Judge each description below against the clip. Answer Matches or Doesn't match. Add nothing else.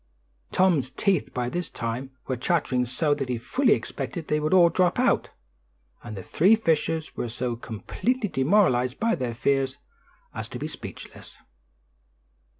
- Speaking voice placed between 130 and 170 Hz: Matches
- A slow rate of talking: Doesn't match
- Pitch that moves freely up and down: Matches